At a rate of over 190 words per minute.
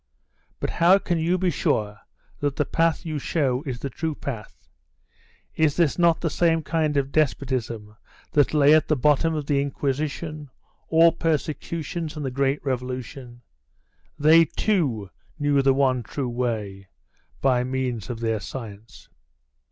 No: average, 150 wpm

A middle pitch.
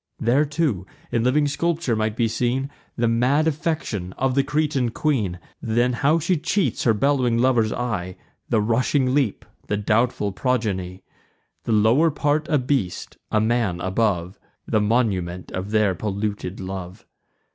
No: low, 115 Hz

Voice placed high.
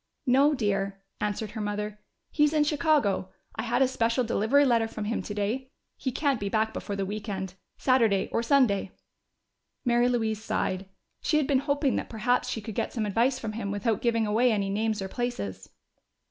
Yes: high, 225 Hz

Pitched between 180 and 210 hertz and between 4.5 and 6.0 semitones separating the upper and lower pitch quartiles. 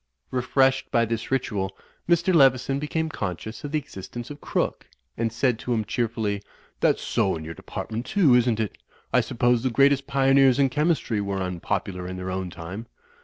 No: low, 120 Hz; average, 5.2 semitones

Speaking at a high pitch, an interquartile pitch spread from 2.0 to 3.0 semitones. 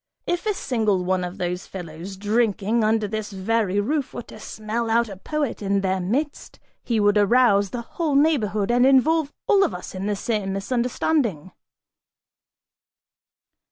No: high, 215 Hz; average, 4.4 semitones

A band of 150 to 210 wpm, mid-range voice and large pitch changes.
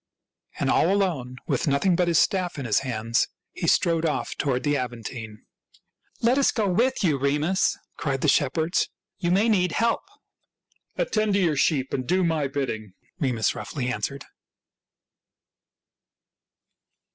Yes: average, 155 wpm; medium, 150 Hz; wide, 6.3 semitones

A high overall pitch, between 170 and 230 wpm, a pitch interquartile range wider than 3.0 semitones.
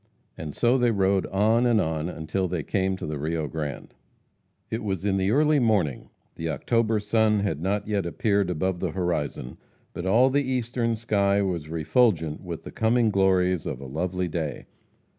No: very low, 95 Hz; average, 180 wpm; average, 5.1 semitones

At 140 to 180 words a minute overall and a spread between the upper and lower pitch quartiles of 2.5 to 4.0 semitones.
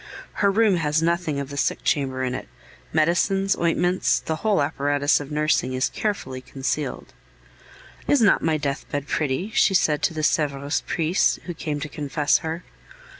Yes: average, 165 wpm; average, 3.5 semitones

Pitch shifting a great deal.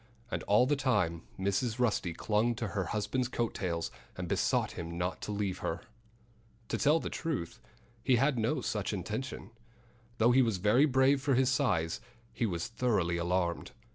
Yes: wide, 6.0 semitones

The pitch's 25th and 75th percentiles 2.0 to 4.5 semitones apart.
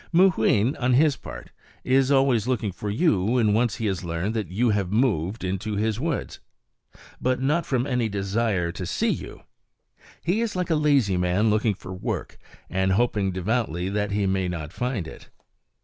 No: average, 5.1 semitones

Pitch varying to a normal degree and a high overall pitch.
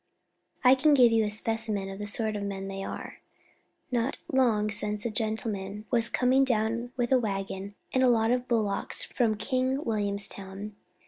Yes: average, 3.1 semitones; high, 220 Hz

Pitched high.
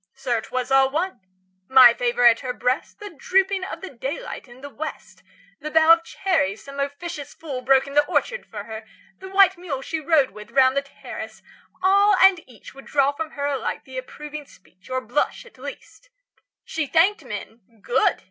Yes: very high, 280 Hz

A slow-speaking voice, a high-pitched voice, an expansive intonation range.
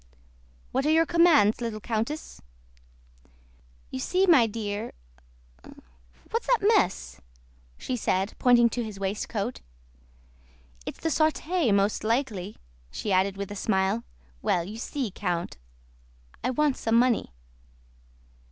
Yes: slow, 120 wpm; high, 225 Hz; wide, 6.3 semitones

